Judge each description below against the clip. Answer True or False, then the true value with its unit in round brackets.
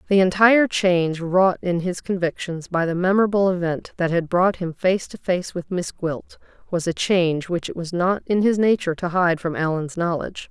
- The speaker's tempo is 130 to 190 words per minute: False (205 wpm)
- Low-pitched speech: False (180 Hz)